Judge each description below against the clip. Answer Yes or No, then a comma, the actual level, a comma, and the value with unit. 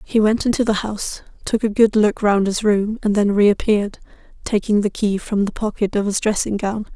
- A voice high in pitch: Yes, high, 210 Hz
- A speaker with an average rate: No, fast, 215 wpm